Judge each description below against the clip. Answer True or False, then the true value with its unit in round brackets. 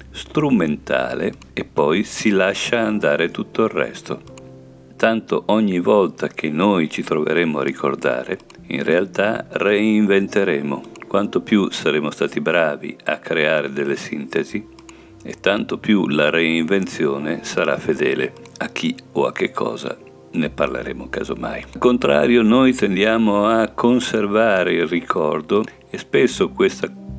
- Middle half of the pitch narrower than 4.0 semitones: False (5.5 semitones)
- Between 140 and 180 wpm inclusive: False (125 wpm)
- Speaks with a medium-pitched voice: False (105 Hz)